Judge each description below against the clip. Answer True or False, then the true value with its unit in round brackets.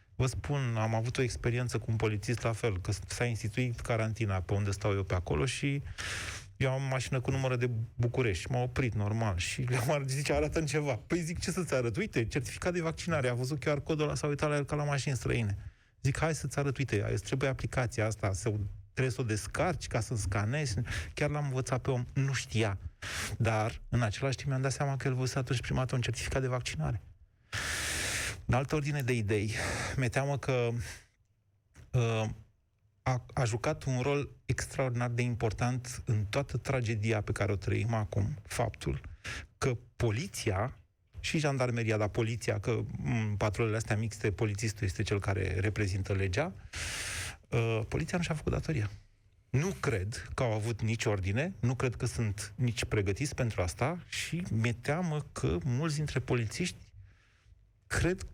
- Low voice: True (115 Hz)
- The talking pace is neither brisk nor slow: False (175 wpm)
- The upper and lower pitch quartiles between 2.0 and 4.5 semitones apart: True (4.1 semitones)